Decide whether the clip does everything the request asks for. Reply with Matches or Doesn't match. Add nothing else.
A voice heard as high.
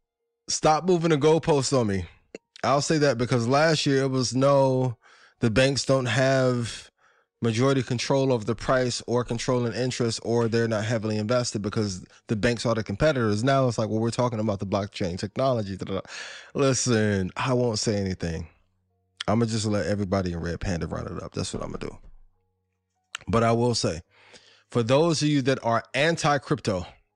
Doesn't match